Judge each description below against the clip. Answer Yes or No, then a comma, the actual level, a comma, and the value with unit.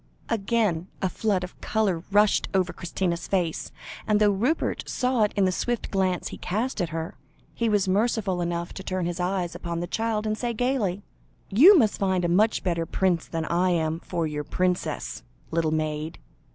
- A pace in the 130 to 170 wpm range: No, average, 185 wpm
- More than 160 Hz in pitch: Yes, medium, 185 Hz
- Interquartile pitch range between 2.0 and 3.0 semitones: No, average, 3.8 semitones